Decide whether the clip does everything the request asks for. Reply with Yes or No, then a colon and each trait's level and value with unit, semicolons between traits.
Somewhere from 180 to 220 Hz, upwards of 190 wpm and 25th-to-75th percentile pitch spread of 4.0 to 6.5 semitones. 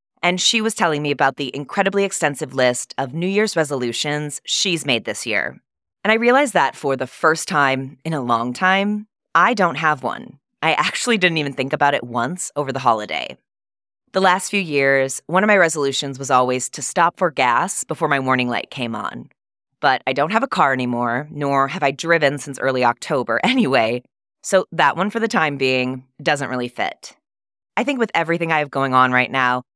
No: medium, 145 Hz; average, 200 wpm; wide, 5.6 semitones